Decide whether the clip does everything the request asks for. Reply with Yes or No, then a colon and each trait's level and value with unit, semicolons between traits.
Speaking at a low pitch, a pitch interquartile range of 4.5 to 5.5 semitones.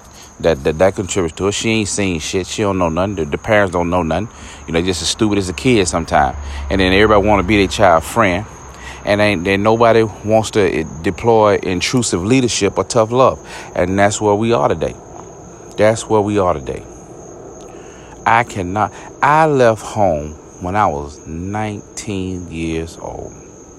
No: low, 100 Hz; average, 3.6 semitones